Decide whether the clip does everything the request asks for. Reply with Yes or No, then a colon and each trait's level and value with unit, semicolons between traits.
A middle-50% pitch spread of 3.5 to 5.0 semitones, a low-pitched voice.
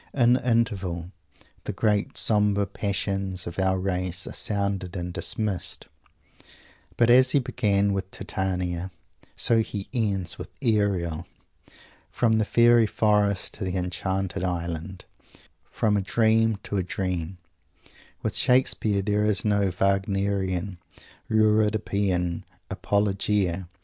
No: narrow, 2.6 semitones; low, 100 Hz